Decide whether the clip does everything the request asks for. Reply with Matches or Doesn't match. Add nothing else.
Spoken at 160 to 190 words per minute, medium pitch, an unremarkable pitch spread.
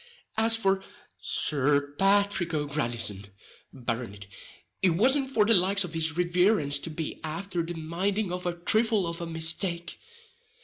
Doesn't match